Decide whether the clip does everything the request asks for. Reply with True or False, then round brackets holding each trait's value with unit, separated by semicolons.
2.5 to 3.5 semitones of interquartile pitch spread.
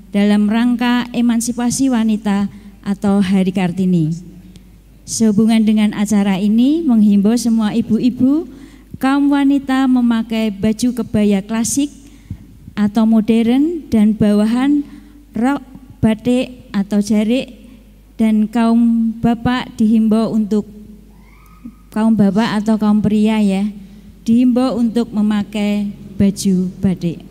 True (2.8 semitones)